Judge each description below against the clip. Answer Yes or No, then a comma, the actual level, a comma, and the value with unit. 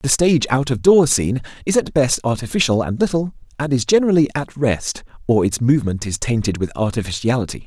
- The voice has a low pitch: Yes, low, 130 Hz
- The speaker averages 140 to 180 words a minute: No, average, 190 wpm